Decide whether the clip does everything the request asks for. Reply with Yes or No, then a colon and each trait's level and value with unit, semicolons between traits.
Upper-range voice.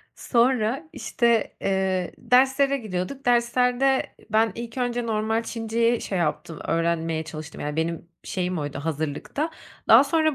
Yes: high, 225 Hz